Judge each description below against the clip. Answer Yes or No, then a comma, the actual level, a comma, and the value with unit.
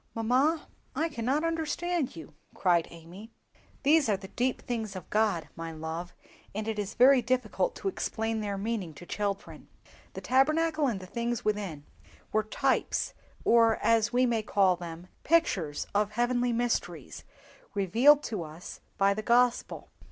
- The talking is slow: No, average, 155 wpm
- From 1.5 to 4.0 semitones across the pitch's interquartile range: No, average, 4.9 semitones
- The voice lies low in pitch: No, high, 220 Hz